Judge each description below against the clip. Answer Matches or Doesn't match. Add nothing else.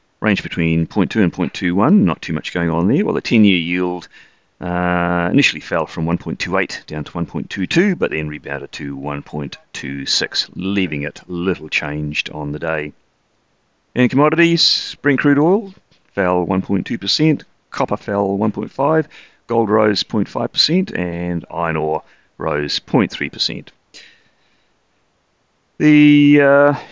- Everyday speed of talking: Doesn't match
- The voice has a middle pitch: Doesn't match